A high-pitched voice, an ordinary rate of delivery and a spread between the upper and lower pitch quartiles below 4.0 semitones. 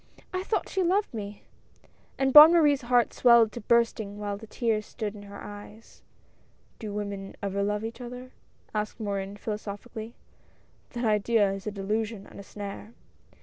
Yes: high, 215 Hz; average, 170 wpm; average, 2.8 semitones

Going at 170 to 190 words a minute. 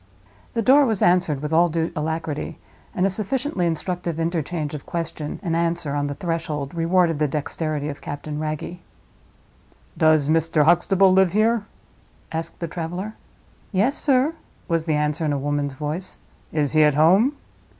No: average, 160 wpm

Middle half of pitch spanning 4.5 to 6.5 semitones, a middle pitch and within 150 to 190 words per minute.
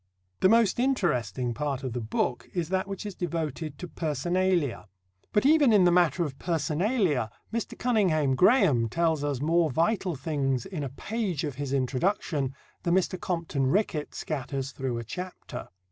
Yes: wide, 5.5 semitones; medium, 160 Hz; average, 160 wpm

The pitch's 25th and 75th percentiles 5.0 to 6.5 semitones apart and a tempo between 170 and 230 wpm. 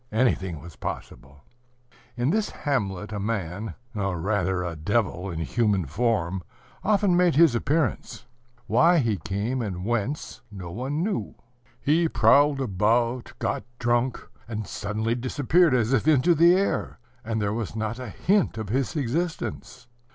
No: wide, 5.6 semitones; average, 145 wpm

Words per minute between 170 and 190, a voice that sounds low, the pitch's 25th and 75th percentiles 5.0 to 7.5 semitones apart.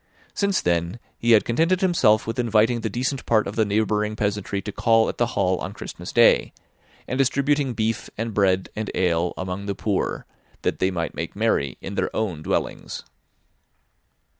No: average, 175 wpm; low, 110 Hz; average, 3.7 semitones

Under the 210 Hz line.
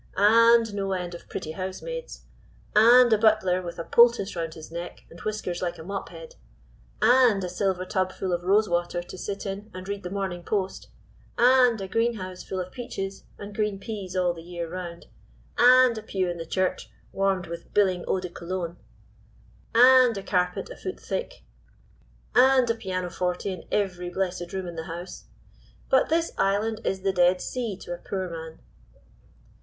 Yes: high, 190 Hz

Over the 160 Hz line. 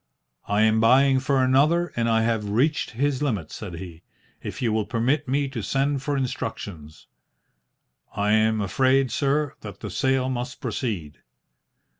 No: low, 120 Hz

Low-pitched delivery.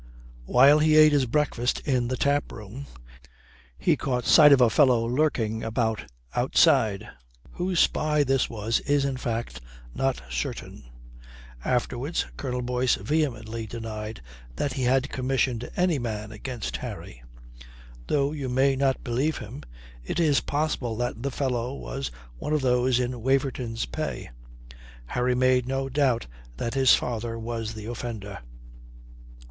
Yes: low, 125 Hz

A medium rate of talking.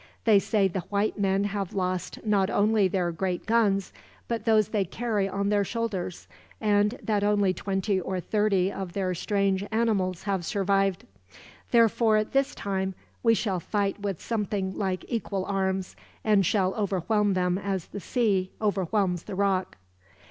Yes: average, 155 wpm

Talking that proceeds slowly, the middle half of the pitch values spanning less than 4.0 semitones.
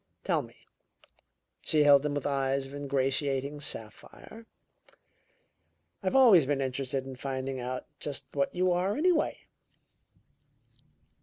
Yes: slow, 125 wpm; average, 2.7 semitones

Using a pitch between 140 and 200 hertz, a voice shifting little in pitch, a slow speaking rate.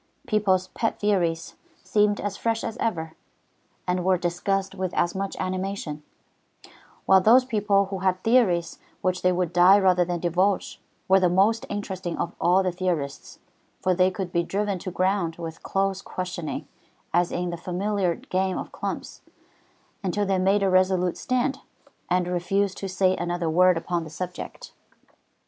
No: medium, 185 Hz; narrow, 2.0 semitones; average, 160 wpm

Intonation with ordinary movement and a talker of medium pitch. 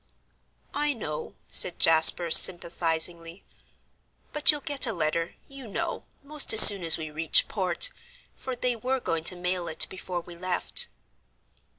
No: wide, 7.0 semitones; medium, 180 Hz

